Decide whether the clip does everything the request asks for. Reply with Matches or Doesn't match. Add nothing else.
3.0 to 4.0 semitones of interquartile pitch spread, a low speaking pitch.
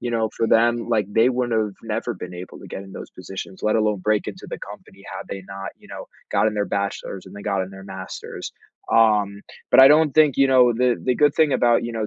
Matches